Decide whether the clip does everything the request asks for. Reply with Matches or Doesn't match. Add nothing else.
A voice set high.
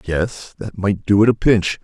Doesn't match